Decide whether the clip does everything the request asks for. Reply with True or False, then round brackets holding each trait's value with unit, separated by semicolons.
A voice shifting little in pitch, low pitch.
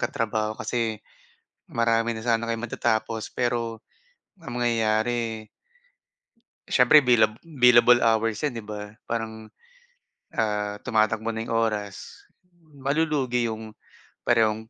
True (1.7 semitones; 115 Hz)